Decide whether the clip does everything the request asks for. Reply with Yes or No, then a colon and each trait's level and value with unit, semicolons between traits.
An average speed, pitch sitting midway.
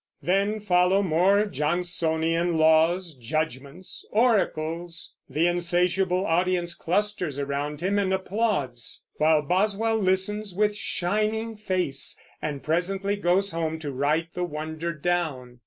No: slow, 115 wpm; medium, 175 Hz